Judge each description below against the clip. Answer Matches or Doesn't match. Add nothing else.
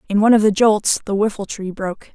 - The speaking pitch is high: Matches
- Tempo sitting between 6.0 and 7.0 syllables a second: Matches